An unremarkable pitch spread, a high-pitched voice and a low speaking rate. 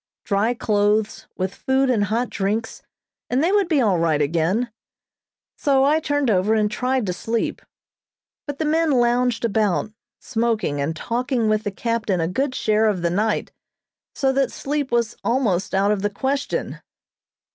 No: average, 4.6 semitones; high, 225 Hz; average, 165 wpm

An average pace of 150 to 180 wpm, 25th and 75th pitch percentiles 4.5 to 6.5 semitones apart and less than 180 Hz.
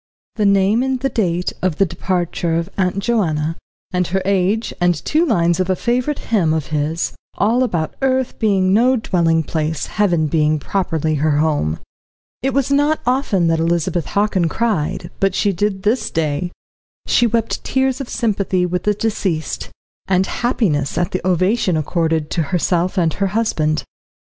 No: average, 165 wpm; average, 5.2 semitones; medium, 185 Hz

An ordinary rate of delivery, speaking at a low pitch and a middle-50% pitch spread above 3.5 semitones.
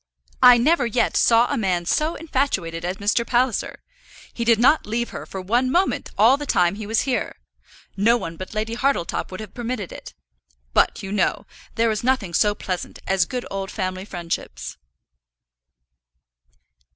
No: average, 165 wpm; high, 220 Hz; average, 4.6 semitones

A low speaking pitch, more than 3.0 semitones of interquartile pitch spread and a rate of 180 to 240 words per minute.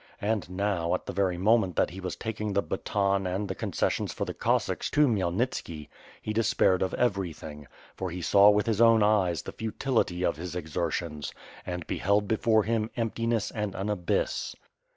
Yes: low, 100 Hz; average, 3.5 semitones; average, 185 wpm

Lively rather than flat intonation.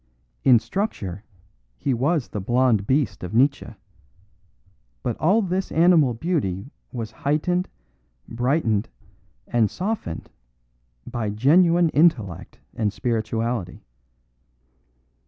Yes: wide, 7.1 semitones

